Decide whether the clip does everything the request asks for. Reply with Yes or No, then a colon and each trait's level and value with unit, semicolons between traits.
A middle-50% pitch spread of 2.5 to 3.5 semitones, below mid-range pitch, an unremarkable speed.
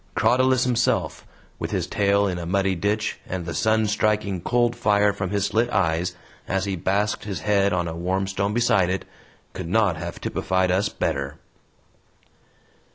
Yes: average, 2.9 semitones; low, 100 Hz; average, 165 wpm